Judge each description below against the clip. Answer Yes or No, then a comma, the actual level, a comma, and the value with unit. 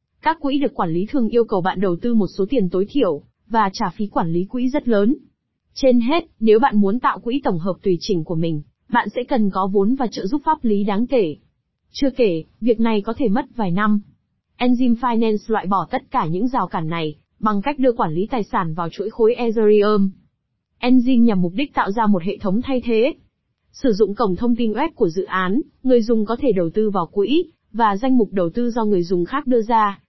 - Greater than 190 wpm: Yes, average, 235 wpm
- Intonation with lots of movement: No, average, 4.3 semitones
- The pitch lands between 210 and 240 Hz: Yes, high, 220 Hz